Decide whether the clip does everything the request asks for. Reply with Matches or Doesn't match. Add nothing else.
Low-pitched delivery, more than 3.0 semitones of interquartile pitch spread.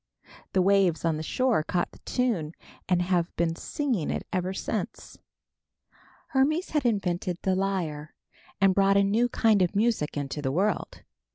Doesn't match